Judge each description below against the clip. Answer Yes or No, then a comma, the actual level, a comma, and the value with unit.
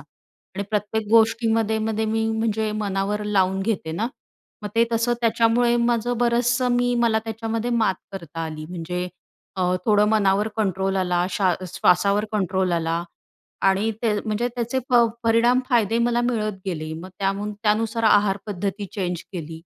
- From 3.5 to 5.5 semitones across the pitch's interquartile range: No, average, 3.0 semitones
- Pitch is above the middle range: Yes, high, 210 Hz